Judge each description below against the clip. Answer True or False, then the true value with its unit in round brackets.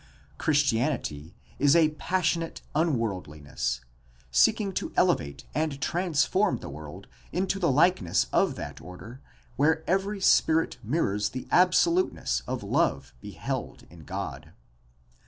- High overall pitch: False (140 Hz)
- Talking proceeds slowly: True (120 wpm)